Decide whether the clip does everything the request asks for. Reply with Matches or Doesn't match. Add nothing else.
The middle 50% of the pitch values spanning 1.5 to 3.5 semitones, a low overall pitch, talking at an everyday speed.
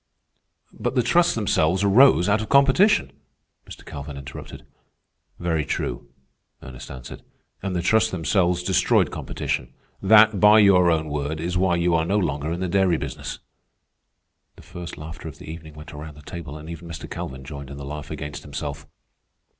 Doesn't match